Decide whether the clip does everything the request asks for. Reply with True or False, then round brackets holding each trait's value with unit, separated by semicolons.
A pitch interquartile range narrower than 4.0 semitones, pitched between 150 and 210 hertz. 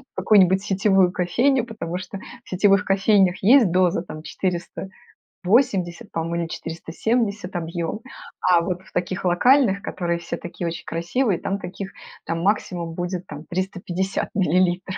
True (2.4 semitones; 185 Hz)